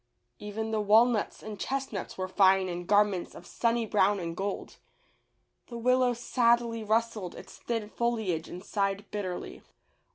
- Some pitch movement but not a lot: Yes, average, 3.2 semitones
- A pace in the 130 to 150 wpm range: Yes, average, 140 wpm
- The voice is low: No, high, 210 Hz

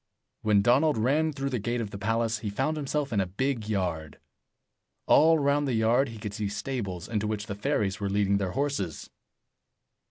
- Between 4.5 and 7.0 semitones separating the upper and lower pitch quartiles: Yes, average, 5.2 semitones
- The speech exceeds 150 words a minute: Yes, average, 190 wpm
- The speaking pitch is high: No, low, 110 Hz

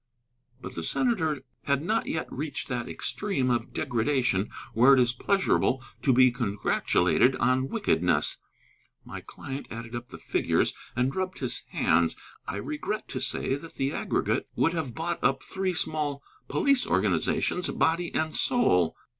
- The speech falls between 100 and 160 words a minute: Yes, average, 150 wpm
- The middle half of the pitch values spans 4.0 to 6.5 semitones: Yes, wide, 5.4 semitones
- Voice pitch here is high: No, low, 135 Hz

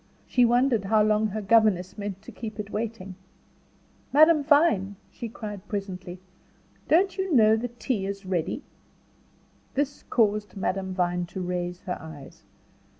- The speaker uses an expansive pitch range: No, average, 3.8 semitones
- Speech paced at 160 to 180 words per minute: No, average, 145 wpm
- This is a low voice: No, high, 210 Hz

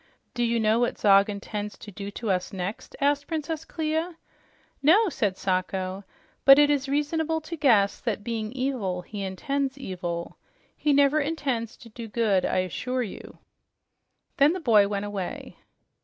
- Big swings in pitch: Yes, wide, 6.2 semitones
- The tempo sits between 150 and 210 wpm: Yes, average, 160 wpm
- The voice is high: Yes, high, 235 Hz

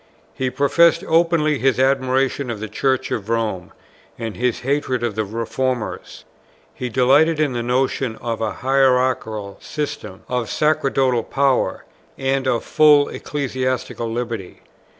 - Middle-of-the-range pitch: No, low, 130 Hz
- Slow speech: Yes, slow, 130 wpm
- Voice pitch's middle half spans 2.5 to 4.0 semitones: Yes, average, 2.9 semitones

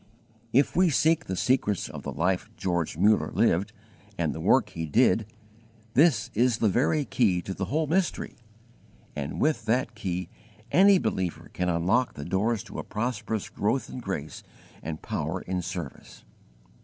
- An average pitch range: No, wide, 6.2 semitones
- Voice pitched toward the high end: No, low, 105 Hz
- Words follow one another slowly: No, average, 160 wpm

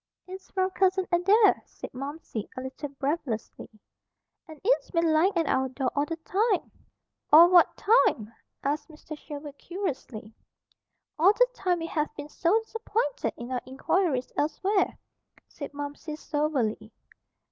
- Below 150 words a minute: Yes, average, 140 wpm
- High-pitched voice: Yes, very high, 310 Hz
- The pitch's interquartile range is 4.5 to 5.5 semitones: Yes, average, 5.1 semitones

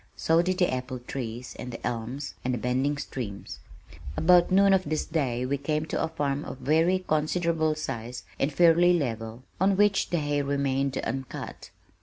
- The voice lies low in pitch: No, medium, 145 Hz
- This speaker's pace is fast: No, average, 175 wpm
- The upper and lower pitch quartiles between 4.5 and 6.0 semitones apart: Yes, average, 4.8 semitones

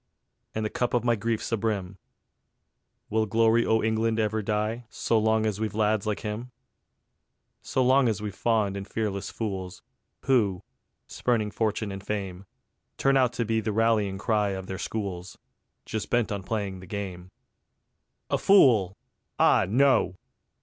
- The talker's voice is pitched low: Yes, low, 110 Hz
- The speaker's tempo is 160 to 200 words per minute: No, average, 150 wpm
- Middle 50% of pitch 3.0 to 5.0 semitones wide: No, narrow, 2.4 semitones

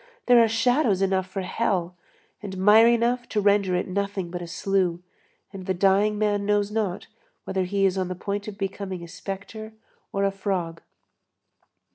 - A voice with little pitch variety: Yes, narrow, 2.0 semitones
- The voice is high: Yes, high, 195 Hz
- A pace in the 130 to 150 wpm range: No, average, 175 wpm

